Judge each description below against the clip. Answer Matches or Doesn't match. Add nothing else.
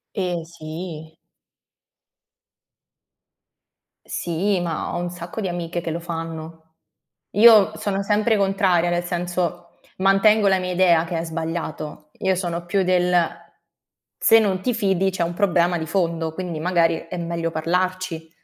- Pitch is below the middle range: Doesn't match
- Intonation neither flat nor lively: Doesn't match